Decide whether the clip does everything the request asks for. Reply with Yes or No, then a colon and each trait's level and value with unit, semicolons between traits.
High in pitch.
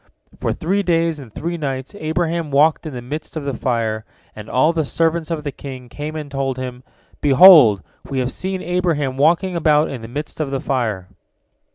No: medium, 145 Hz